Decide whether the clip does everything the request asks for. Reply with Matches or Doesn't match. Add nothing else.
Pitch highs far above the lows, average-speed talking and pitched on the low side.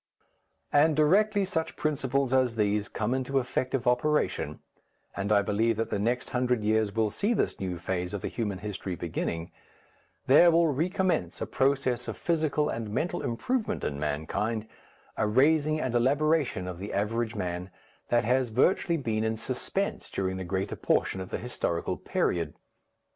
Matches